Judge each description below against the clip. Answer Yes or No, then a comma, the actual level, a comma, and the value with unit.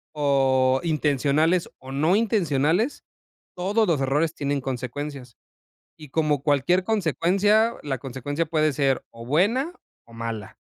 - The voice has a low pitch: No, medium, 150 Hz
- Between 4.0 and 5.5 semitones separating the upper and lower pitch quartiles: Yes, average, 4.9 semitones